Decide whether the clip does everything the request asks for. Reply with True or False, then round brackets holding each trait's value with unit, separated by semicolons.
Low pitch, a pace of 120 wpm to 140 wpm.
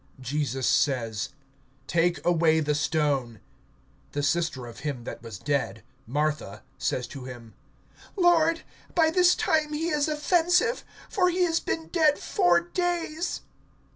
False (165 Hz; 135 wpm)